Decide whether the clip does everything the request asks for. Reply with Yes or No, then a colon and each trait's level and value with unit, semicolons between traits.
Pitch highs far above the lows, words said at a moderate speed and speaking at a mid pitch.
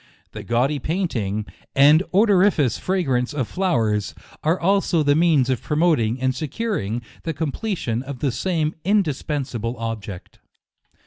No: wide, 6.4 semitones; slow, 130 wpm; medium, 145 Hz